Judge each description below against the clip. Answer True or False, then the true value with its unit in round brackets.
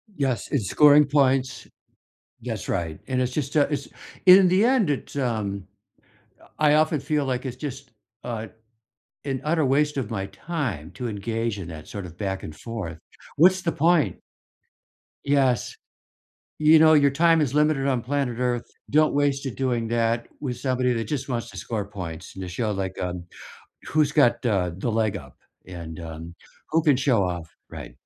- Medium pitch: False (125 Hz)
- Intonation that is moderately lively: False (6.3 semitones)